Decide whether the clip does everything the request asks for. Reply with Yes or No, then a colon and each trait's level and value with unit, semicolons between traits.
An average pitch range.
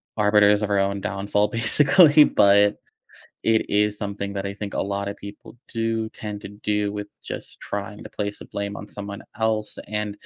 No: narrow, 1.0 semitones